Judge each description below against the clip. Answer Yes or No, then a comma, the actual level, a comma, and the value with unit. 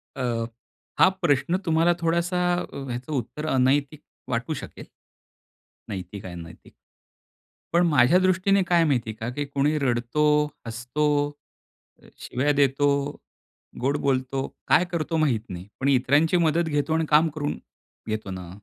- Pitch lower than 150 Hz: Yes, medium, 140 Hz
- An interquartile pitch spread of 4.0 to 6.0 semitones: Yes, average, 5.0 semitones